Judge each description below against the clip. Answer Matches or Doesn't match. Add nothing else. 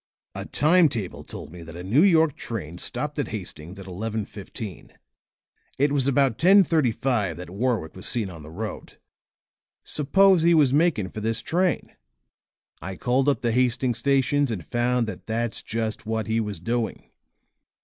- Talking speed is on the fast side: Doesn't match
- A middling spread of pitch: Doesn't match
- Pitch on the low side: Matches